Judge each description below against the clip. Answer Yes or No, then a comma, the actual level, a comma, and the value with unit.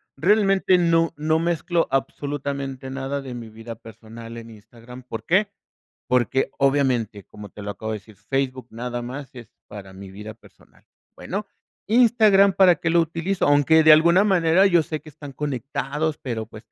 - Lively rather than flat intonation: Yes, wide, 6.2 semitones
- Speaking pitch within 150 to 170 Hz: No, low, 135 Hz